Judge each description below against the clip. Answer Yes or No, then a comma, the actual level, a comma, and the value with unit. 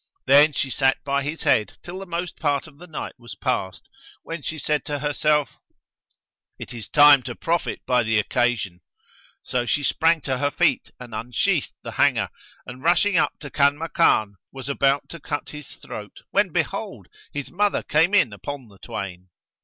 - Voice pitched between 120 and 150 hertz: Yes, medium, 140 Hz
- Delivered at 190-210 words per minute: No, average, 175 wpm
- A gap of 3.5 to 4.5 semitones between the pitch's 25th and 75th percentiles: Yes, average, 4.2 semitones